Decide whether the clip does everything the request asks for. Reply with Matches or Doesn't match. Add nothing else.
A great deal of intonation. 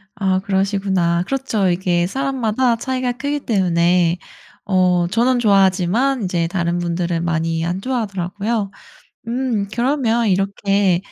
Doesn't match